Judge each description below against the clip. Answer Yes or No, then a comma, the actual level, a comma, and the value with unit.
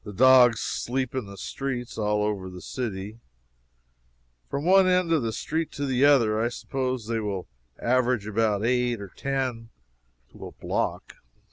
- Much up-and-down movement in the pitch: No, average, 3.8 semitones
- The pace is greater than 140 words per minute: Yes, average, 160 wpm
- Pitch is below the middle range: Yes, low, 120 Hz